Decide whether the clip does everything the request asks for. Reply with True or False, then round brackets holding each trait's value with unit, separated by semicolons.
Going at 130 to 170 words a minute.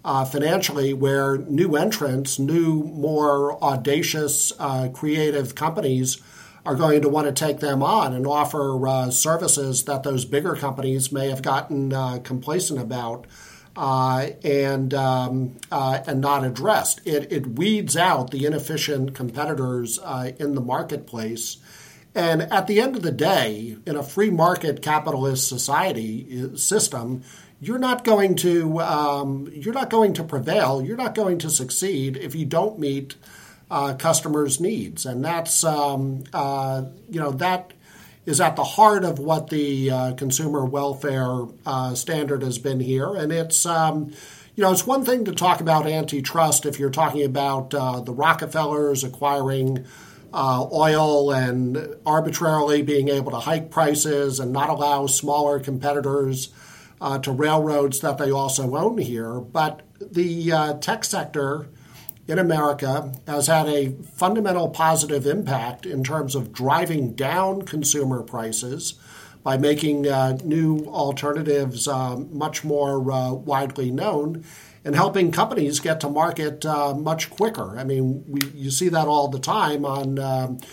True (150 wpm)